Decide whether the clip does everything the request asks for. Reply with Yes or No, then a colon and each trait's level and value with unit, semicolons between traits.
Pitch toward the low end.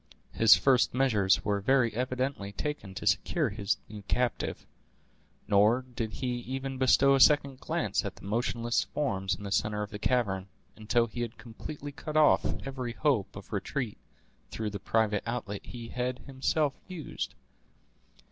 Yes: low, 120 Hz